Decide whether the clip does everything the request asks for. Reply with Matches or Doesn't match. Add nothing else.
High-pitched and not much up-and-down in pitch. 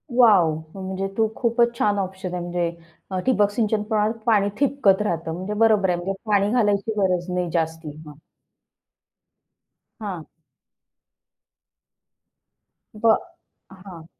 Doesn't match